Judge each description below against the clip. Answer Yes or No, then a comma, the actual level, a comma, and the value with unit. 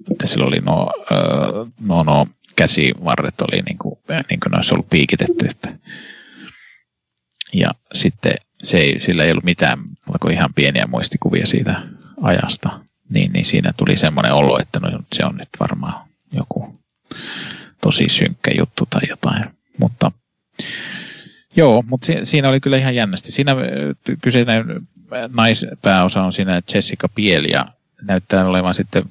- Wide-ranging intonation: Yes, wide, 6.1 semitones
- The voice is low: Yes, low, 110 Hz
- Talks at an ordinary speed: Yes, average, 135 wpm